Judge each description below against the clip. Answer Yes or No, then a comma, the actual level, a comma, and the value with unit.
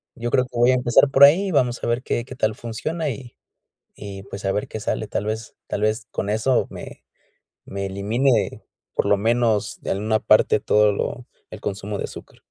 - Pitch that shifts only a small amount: No, average, 3.1 semitones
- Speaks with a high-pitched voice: No, low, 110 Hz